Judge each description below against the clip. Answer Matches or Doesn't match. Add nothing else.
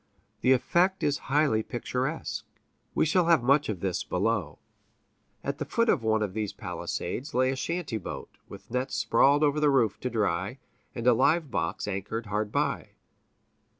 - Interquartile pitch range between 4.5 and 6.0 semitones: Matches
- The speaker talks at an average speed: Matches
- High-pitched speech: Doesn't match